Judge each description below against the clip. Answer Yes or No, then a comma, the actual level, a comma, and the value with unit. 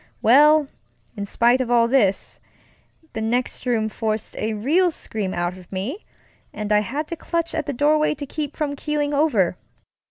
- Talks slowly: No, average, 170 wpm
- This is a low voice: No, very high, 250 Hz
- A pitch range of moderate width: No, wide, 5.8 semitones